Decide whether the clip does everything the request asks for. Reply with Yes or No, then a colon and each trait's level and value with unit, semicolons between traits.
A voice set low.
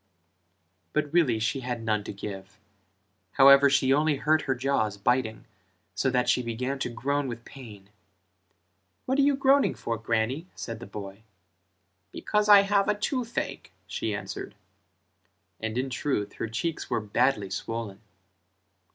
Yes: low, 125 Hz